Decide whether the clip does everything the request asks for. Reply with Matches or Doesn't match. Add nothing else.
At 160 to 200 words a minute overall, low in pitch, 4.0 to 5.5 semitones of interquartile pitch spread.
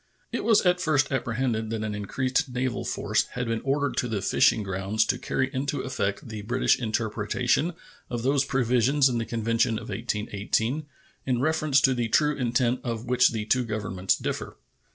Doesn't match